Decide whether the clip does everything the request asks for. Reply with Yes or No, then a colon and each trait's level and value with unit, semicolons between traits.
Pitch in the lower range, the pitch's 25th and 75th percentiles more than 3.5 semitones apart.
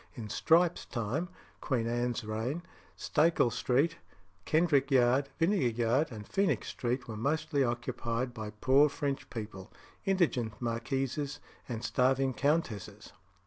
Yes: low, 130 Hz; average, 4.2 semitones